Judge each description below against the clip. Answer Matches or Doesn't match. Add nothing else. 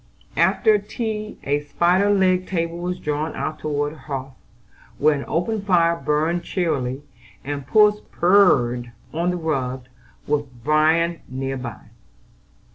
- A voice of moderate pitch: Matches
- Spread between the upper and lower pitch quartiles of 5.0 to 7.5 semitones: Doesn't match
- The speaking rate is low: Matches